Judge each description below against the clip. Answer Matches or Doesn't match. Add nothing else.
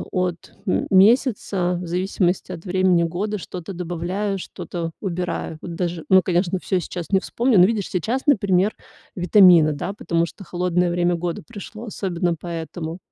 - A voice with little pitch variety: Matches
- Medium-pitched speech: Matches